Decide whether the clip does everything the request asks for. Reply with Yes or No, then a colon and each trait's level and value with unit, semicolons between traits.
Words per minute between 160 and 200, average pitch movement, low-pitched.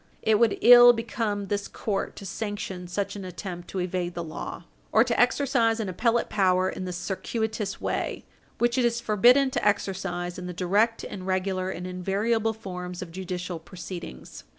No: average, 175 wpm; average, 3.7 semitones; high, 195 Hz